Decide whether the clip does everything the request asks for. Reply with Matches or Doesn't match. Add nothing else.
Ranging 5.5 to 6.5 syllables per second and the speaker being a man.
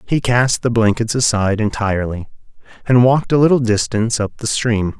Matches